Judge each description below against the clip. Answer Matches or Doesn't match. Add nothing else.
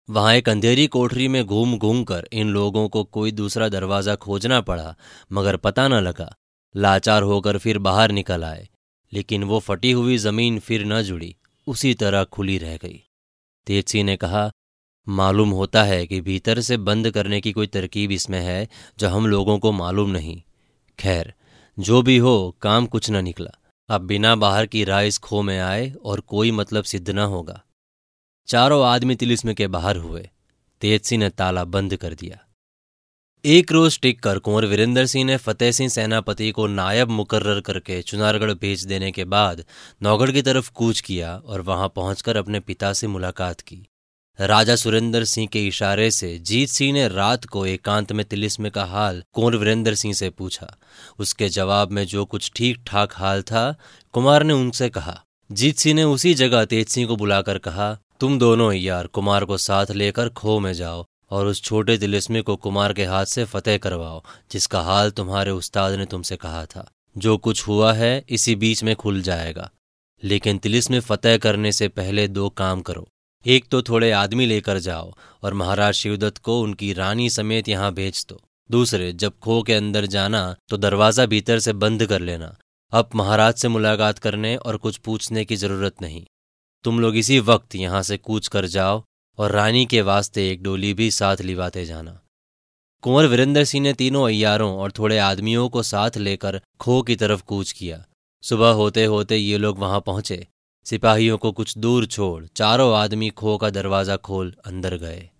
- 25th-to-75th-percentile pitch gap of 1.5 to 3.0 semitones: Matches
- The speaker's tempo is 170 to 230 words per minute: Matches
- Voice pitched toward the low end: Matches